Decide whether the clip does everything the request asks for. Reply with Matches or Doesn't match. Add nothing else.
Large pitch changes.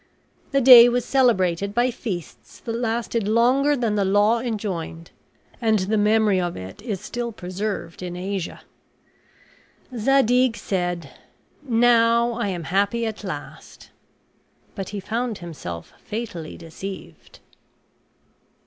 Doesn't match